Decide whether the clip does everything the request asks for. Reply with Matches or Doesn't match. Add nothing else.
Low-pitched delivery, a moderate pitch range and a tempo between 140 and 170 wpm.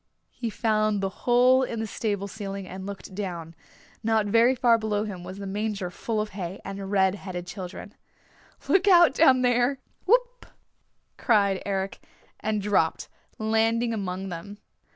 Doesn't match